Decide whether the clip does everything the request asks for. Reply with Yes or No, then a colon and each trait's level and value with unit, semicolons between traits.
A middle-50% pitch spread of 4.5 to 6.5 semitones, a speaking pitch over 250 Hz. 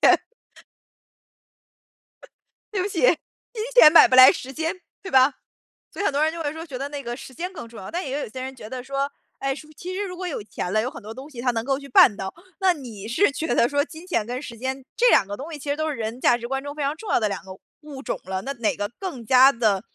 Yes: average, 4.8 semitones; very high, 270 Hz